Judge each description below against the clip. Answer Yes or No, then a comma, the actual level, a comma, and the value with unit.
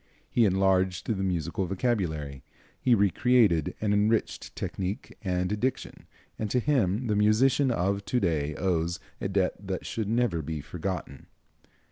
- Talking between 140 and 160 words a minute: Yes, average, 145 wpm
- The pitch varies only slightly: No, average, 3.9 semitones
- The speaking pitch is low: Yes, very low, 95 Hz